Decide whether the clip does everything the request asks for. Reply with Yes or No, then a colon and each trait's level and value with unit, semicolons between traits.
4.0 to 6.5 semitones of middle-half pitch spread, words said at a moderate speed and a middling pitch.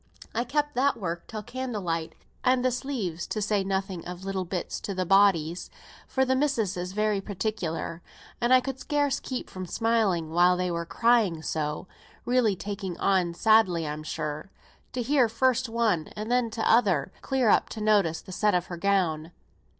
No: average, 5.2 semitones; average, 175 wpm; high, 200 Hz